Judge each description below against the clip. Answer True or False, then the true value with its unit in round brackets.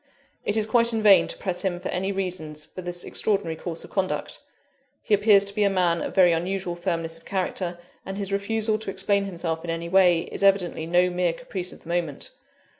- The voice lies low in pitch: False (185 Hz)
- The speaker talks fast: True (215 wpm)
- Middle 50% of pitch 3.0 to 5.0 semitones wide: False (2.6 semitones)